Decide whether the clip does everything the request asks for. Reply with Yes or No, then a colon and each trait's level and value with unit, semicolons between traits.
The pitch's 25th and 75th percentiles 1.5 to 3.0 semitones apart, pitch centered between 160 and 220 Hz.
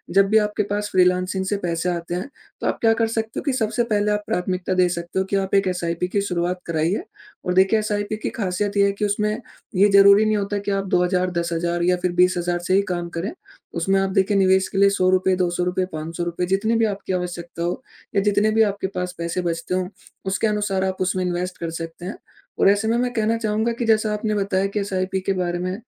Yes: narrow, 2.5 semitones; high, 190 Hz